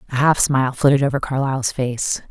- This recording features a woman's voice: Yes, female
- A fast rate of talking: No, average, 185 wpm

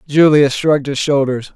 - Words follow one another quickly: No, average, 155 wpm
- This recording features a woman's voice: No, male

